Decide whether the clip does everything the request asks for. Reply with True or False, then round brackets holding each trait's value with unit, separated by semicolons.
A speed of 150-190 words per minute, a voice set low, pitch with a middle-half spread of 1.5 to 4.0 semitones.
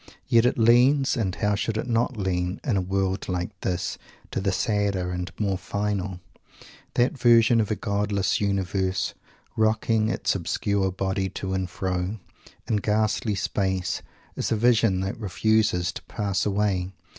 True (155 wpm; 100 Hz; 2.7 semitones)